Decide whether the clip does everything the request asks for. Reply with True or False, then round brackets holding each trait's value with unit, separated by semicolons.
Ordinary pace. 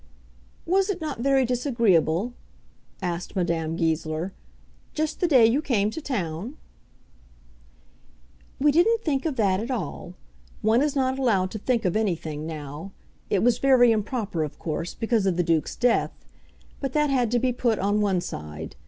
True (160 wpm)